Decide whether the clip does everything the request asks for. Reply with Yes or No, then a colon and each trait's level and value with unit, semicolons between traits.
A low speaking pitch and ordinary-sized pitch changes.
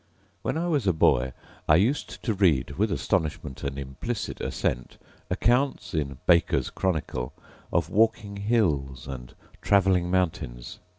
No: very low, 85 Hz; wide, 7.4 semitones